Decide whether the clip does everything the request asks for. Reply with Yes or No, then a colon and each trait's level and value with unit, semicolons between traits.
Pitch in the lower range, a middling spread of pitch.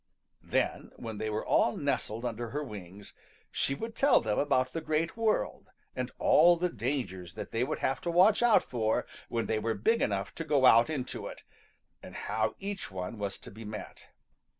No: low, 120 Hz; wide, 6.7 semitones